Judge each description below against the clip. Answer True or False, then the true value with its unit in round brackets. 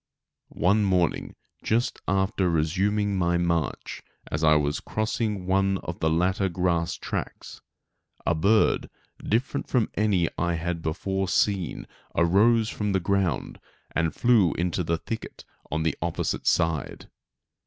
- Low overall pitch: True (90 Hz)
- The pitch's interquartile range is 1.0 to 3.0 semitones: False (3.5 semitones)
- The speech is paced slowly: True (130 wpm)